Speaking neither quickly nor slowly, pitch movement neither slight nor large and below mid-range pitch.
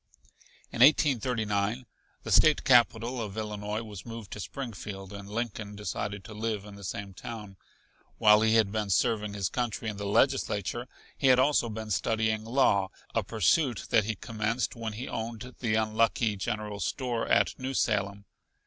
No: average, 165 wpm; narrow, 2.3 semitones; low, 110 Hz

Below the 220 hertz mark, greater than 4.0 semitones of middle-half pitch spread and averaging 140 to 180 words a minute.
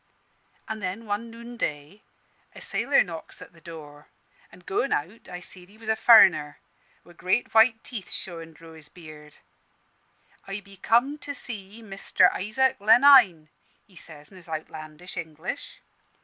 Yes: high, 190 Hz; wide, 5.5 semitones; average, 150 wpm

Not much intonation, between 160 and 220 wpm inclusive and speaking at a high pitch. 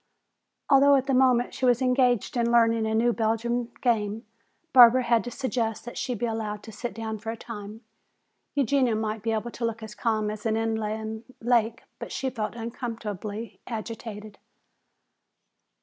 Yes: narrow, 1.9 semitones; average, 165 wpm; high, 230 Hz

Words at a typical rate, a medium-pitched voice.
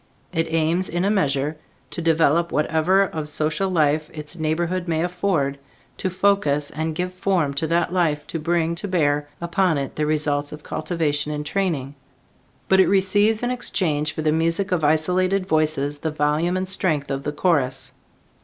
Yes: average, 170 wpm; medium, 160 Hz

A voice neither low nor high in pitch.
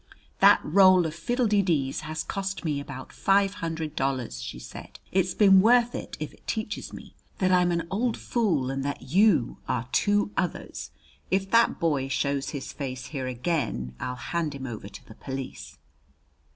Yes: medium, 160 Hz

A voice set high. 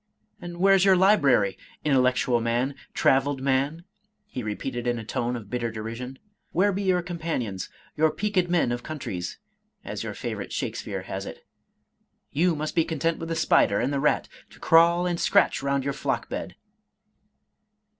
No: medium, 140 Hz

